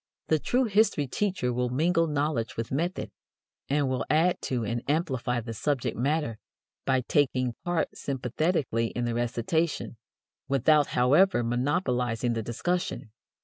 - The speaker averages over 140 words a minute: No, slow, 135 wpm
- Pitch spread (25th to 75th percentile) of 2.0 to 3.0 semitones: No, average, 4.8 semitones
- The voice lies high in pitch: No, low, 135 Hz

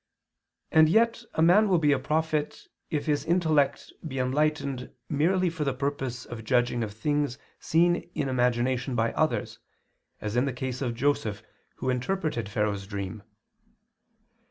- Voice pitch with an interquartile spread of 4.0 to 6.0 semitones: Yes, average, 4.5 semitones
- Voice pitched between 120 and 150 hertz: Yes, low, 135 Hz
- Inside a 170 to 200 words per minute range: No, average, 150 wpm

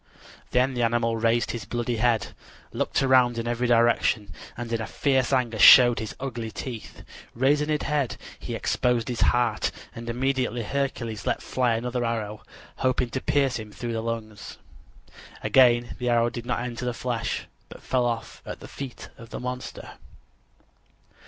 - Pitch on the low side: Yes, low, 120 Hz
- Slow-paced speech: No, average, 160 wpm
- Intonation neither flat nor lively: No, narrow, 1.7 semitones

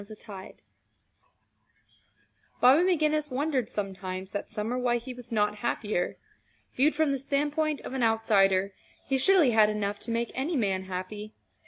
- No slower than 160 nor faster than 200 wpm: No, average, 150 wpm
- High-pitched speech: Yes, high, 230 Hz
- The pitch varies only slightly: No, average, 5.1 semitones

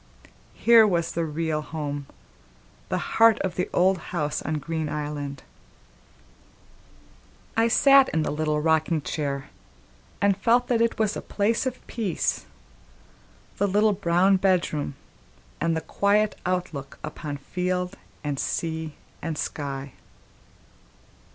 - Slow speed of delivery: Yes, slow, 120 wpm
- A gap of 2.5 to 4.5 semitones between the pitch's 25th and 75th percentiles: No, average, 4.9 semitones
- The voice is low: No, medium, 170 Hz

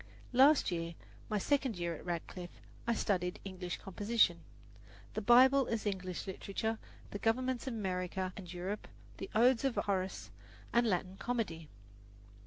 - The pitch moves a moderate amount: Yes, average, 4.5 semitones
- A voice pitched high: Yes, high, 200 Hz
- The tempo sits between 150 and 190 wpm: No, average, 140 wpm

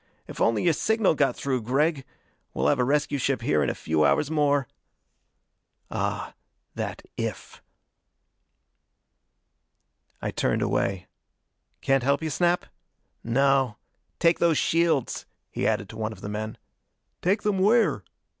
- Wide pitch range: Yes, wide, 6.3 semitones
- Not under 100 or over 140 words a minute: Yes, slow, 135 wpm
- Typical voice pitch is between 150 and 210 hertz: No, medium, 140 Hz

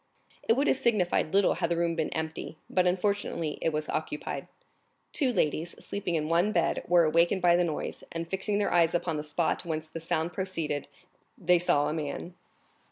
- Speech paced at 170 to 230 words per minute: Yes, average, 190 wpm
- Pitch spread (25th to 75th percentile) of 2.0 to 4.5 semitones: Yes, narrow, 2.5 semitones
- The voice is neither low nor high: Yes, medium, 170 Hz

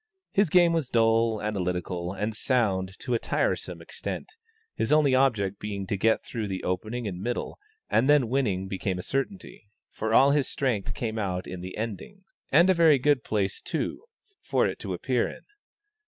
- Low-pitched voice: Yes, low, 110 Hz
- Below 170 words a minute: No, average, 180 wpm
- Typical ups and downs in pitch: No, wide, 6.0 semitones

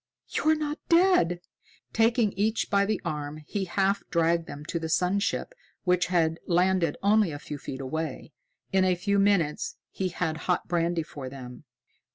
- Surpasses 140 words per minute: Yes, average, 170 wpm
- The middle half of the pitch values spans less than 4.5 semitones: Yes, average, 3.9 semitones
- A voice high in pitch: No, medium, 180 Hz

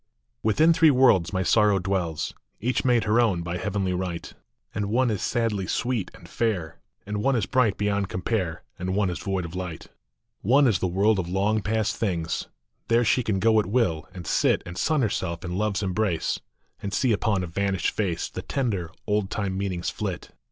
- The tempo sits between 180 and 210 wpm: Yes, average, 195 wpm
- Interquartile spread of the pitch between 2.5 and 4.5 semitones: Yes, average, 3.5 semitones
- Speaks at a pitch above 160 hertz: No, low, 100 Hz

